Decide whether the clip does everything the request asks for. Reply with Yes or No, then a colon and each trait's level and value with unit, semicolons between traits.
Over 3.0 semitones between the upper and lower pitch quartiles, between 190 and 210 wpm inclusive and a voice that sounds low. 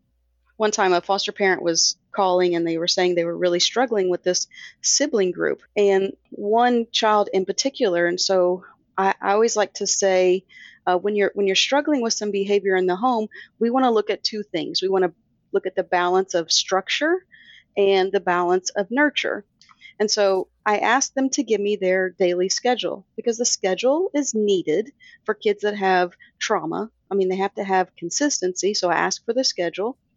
No: average, 3.8 semitones; average, 195 wpm; high, 195 Hz